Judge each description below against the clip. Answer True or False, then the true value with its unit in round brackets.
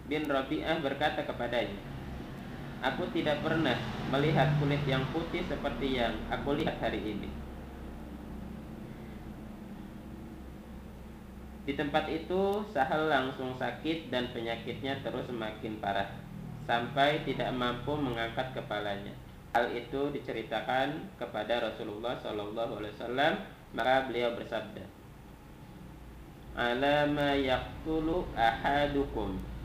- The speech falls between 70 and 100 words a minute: True (90 wpm)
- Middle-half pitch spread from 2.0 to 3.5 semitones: False (4.2 semitones)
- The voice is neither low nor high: False (130 Hz)